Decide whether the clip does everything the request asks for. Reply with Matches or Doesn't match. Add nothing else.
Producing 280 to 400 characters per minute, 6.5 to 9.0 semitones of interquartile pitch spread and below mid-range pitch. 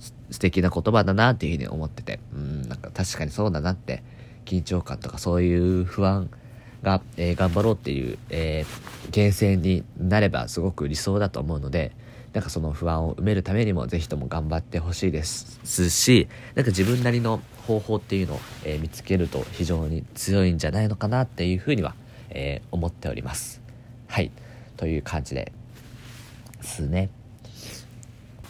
Doesn't match